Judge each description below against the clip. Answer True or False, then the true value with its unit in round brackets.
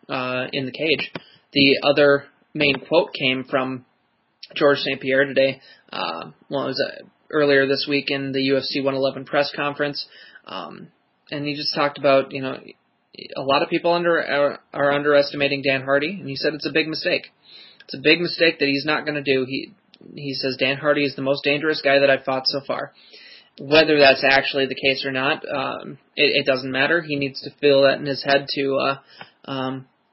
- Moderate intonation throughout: False (1.3 semitones)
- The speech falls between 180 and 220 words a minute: True (200 wpm)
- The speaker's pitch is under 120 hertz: False (140 Hz)